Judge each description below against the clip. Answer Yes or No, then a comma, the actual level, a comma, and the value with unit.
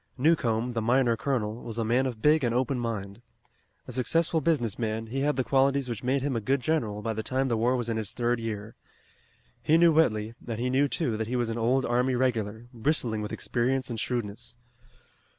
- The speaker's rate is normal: No, fast, 215 wpm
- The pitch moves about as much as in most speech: Yes, average, 3.0 semitones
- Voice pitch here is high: No, low, 120 Hz